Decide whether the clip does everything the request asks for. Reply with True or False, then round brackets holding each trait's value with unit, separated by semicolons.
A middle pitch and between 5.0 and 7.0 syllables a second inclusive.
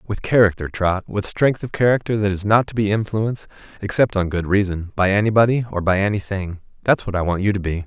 False (100 Hz; 5.9 syllables/s)